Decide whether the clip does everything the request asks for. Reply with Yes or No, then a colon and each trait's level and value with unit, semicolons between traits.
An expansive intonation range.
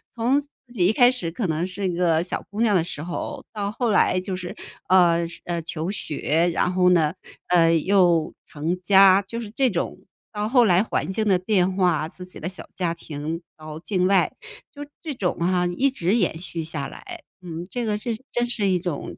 No: average, 3.7 semitones